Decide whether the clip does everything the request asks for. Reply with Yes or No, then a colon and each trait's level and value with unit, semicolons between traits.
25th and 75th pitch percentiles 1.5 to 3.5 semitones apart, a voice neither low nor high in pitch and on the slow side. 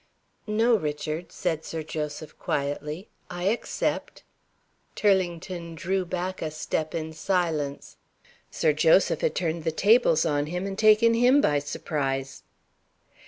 No: average, 4.2 semitones; medium, 170 Hz; slow, 130 wpm